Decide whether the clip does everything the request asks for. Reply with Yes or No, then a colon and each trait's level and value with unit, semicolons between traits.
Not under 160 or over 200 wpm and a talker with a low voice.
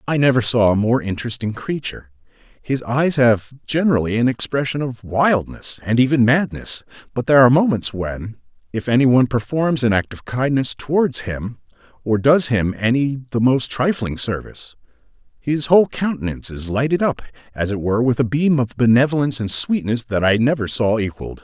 Yes: average, 170 wpm; low, 125 Hz